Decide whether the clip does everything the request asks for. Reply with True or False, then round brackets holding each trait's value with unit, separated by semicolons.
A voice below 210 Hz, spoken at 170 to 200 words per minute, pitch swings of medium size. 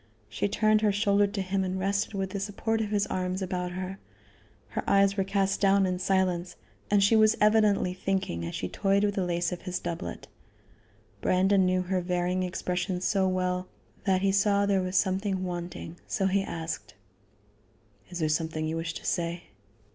False (190 Hz; 185 wpm; 1.7 semitones)